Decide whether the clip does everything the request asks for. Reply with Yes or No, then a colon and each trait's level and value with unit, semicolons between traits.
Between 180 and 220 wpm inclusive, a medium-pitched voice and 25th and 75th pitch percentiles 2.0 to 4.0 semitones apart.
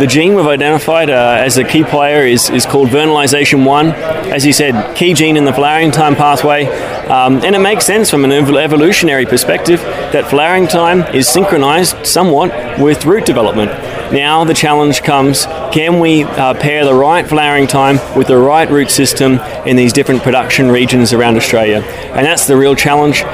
Yes: average, 185 wpm; medium, 145 Hz; average, 3.0 semitones